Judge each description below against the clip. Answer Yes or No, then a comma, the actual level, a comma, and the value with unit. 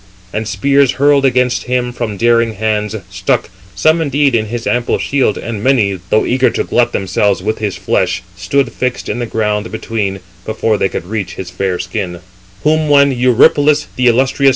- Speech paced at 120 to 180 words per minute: Yes, average, 155 wpm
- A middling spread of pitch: Yes, average, 4.1 semitones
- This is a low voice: Yes, low, 110 Hz